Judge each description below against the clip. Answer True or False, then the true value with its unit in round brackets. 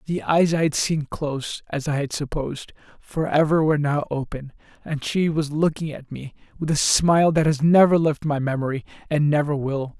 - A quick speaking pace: False (190 wpm)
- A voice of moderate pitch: True (150 Hz)